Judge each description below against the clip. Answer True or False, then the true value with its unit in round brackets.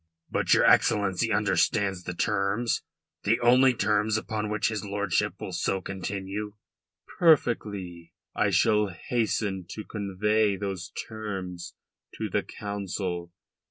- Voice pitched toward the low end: True (100 Hz)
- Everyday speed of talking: False (120 wpm)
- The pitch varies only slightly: True (2.2 semitones)